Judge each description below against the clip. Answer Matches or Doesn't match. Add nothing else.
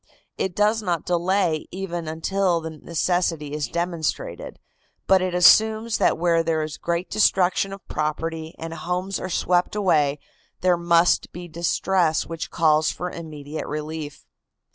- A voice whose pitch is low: Doesn't match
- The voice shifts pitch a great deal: Doesn't match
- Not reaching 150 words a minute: Matches